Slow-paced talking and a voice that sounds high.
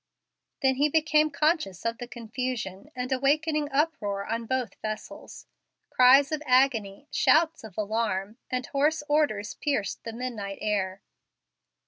Yes: slow, 130 wpm; very high, 250 Hz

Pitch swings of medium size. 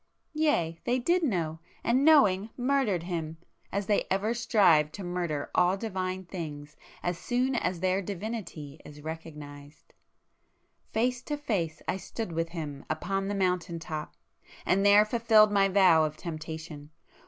Yes: average, 5.0 semitones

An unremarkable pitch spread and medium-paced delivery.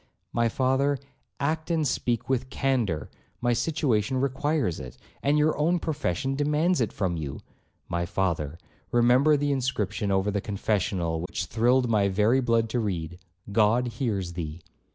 No: wide, 6.0 semitones; average, 150 wpm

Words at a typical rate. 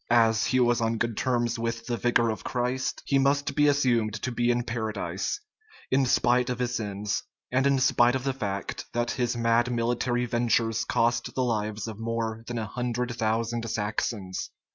Yes: average, 185 wpm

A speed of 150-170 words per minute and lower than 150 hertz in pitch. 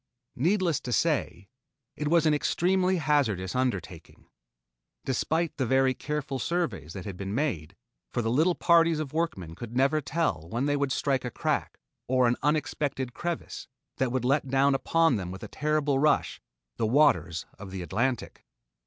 Yes: average, 165 wpm; low, 135 Hz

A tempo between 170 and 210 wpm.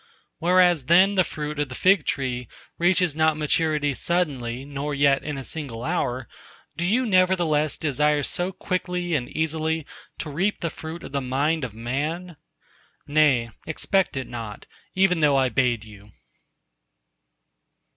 No: average, 145 wpm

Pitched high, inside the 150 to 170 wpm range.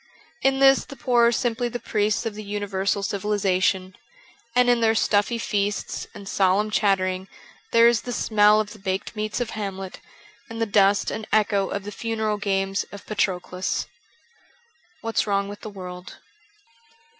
Yes: high, 210 Hz; average, 165 wpm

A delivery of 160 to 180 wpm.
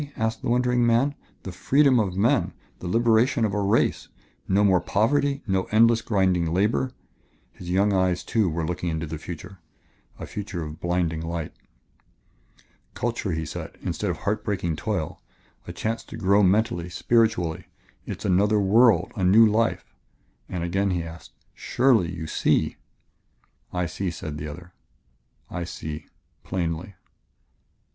No: average, 150 wpm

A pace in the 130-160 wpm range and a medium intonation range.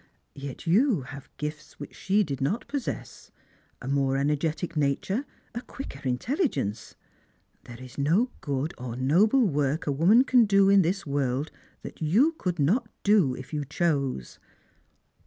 No: average, 155 wpm; wide, 6.6 semitones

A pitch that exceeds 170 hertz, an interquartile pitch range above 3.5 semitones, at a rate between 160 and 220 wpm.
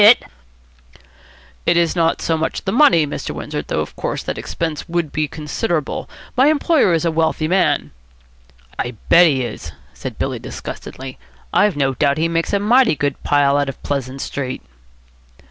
No: medium, 155 Hz; average, 4.2 semitones; average, 165 wpm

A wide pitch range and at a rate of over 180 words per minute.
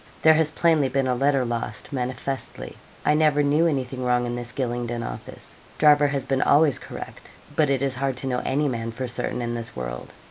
No: average, 3.0 semitones; fast, 205 wpm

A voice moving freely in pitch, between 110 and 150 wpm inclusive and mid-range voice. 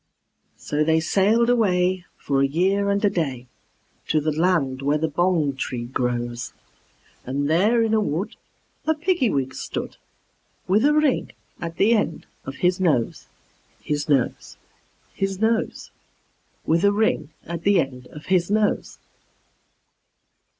Yes: wide, 6.0 semitones; average, 140 wpm; medium, 170 Hz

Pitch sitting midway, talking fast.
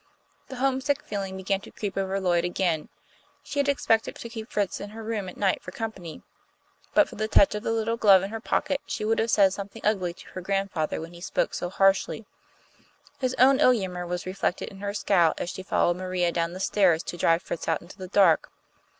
No: high, 195 Hz; fast, 220 wpm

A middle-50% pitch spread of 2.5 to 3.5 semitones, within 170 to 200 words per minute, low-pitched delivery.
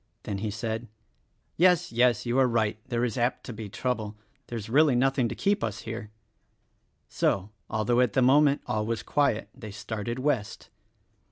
Yes: average, 3.2 semitones; average, 180 wpm; low, 120 Hz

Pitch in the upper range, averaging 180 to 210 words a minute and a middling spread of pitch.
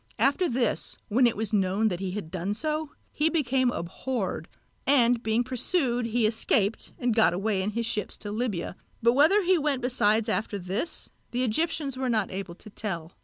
Yes: high, 230 Hz; average, 185 wpm; average, 4.3 semitones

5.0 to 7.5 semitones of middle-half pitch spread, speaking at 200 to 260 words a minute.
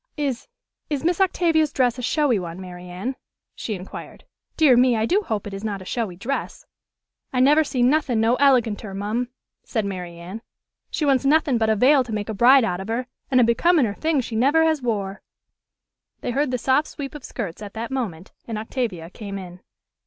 Yes: average, 5.3 semitones; fast, 205 wpm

